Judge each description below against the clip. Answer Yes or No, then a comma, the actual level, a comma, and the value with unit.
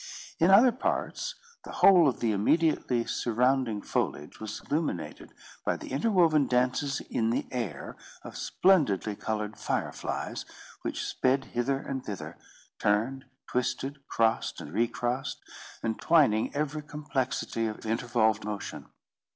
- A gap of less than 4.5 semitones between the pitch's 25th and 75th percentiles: No, average, 4.8 semitones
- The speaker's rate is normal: No, slow, 125 wpm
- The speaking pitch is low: Yes, low, 125 Hz